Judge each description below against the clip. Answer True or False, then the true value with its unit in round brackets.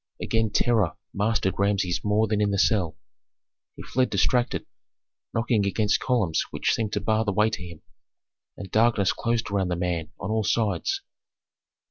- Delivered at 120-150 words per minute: False (160 wpm)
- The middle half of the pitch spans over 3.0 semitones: False (2.6 semitones)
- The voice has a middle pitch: False (105 Hz)